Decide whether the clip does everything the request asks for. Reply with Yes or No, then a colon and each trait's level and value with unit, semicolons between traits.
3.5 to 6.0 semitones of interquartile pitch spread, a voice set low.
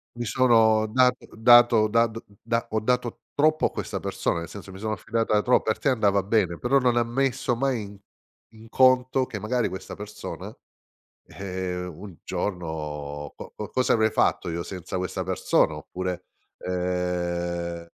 Yes: average, 5.0 semitones; low, 105 Hz